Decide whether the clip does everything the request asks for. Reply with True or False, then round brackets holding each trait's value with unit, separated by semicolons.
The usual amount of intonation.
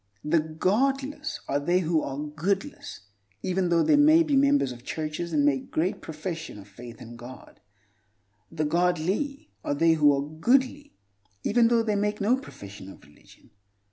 False (8.4 semitones)